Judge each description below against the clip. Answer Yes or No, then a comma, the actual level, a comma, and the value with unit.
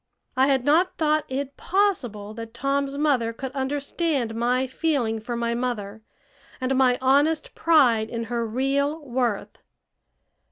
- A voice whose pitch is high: Yes, very high, 260 Hz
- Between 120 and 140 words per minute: Yes, slow, 135 wpm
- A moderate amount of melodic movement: Yes, average, 3.6 semitones